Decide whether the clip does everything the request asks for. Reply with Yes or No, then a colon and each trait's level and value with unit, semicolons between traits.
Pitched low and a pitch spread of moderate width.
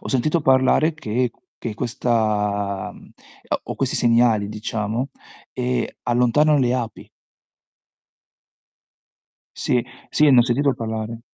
Yes: low, 120 Hz; average, 3.0 semitones